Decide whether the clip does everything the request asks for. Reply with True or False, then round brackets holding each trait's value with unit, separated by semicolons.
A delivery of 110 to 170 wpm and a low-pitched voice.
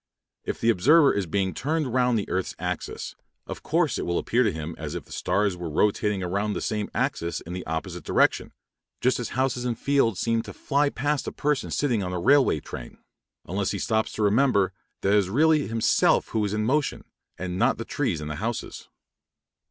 False (205 wpm; 110 Hz)